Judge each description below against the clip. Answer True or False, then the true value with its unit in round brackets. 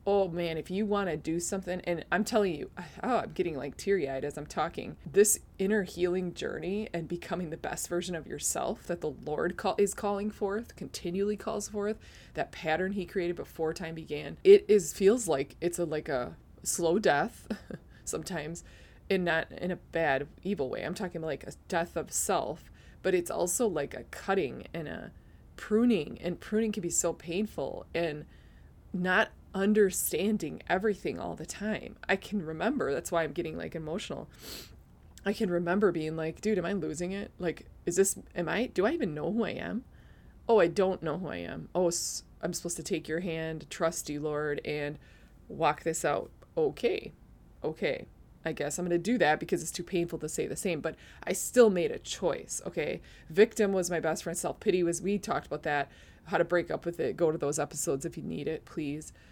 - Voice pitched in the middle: True (175 Hz)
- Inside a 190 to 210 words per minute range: True (200 wpm)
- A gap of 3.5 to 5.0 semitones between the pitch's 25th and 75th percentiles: True (3.9 semitones)